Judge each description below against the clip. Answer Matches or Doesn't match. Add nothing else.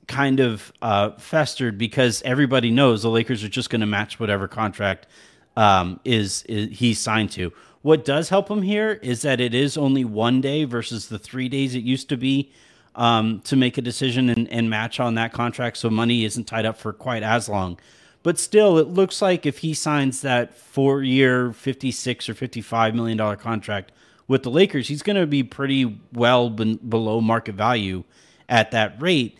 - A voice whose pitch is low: Matches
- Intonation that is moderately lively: Matches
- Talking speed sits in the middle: Matches